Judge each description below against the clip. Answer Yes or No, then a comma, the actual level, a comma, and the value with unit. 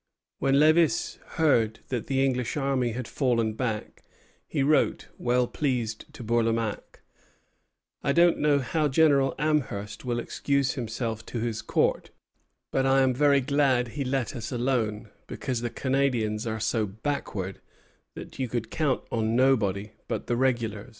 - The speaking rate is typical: Yes, average, 150 wpm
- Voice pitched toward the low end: Yes, low, 125 Hz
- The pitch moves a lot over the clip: No, average, 3.5 semitones